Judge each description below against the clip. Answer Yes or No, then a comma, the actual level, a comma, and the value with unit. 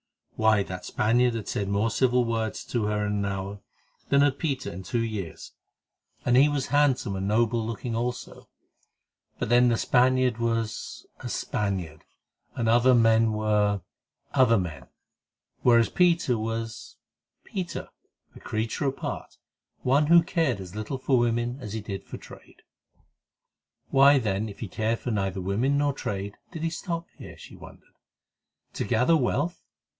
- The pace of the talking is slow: No, average, 150 wpm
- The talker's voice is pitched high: No, low, 115 Hz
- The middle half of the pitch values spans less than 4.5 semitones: Yes, average, 3.8 semitones